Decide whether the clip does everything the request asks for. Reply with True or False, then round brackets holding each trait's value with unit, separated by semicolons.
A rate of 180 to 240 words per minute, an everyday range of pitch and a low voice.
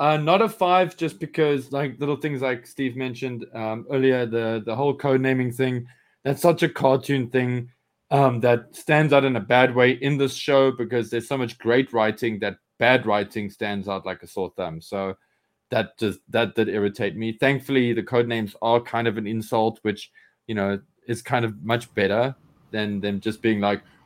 True (200 wpm; 3.5 semitones; 120 Hz)